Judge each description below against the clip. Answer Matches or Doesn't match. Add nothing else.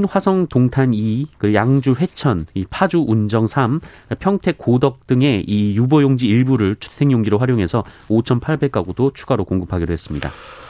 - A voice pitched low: Matches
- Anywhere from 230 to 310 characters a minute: Matches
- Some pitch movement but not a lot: Matches